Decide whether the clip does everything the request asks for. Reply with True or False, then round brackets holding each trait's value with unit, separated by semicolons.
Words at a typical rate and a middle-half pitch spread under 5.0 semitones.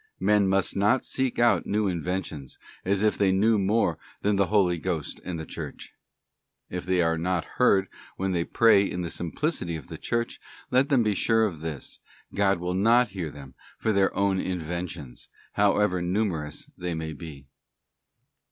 True (170 wpm; 3.6 semitones)